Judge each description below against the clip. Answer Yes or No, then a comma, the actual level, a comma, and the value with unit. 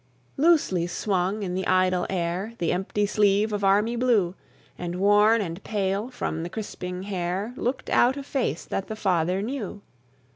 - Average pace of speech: Yes, average, 160 wpm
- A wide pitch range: No, average, 3.2 semitones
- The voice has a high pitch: Yes, high, 195 Hz